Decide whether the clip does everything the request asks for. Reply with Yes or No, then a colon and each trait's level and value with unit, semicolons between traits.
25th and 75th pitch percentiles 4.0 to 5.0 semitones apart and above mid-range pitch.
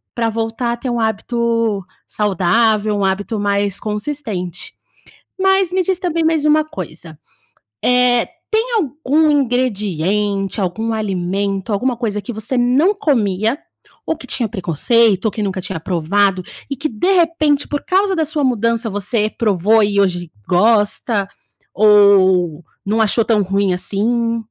Yes: average, 4.5 semitones; high, 220 Hz